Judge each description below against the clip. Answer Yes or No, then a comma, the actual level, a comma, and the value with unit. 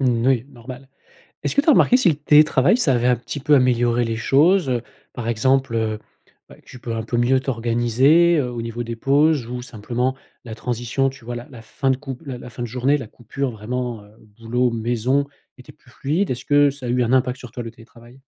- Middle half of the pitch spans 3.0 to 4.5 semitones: No, narrow, 2.4 semitones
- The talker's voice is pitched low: Yes, low, 125 Hz